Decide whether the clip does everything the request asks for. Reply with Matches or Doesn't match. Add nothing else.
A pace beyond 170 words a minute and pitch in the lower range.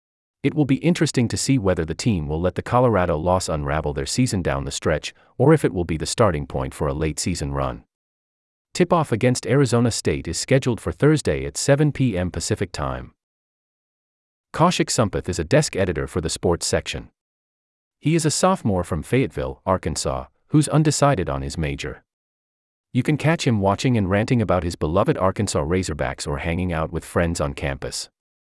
Matches